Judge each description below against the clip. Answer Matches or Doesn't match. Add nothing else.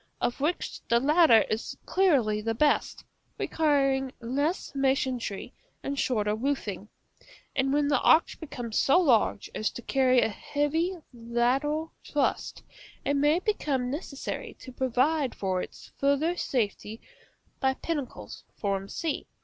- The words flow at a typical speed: Doesn't match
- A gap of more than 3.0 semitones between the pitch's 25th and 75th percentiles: Matches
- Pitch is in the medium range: Doesn't match